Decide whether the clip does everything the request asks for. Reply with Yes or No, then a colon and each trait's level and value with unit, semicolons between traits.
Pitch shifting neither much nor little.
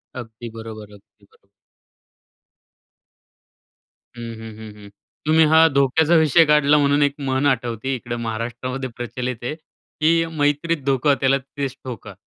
Yes: average, 4.2 semitones